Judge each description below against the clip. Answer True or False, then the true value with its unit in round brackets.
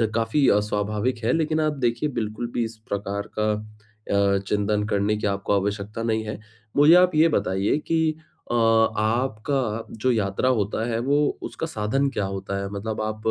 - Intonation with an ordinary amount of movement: True (3.8 semitones)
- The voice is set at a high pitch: False (110 Hz)